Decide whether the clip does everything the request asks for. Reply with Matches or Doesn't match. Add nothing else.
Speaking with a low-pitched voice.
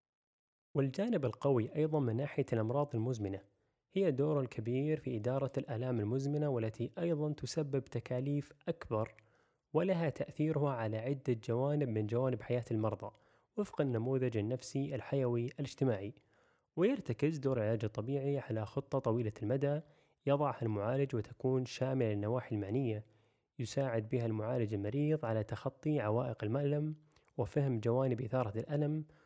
Matches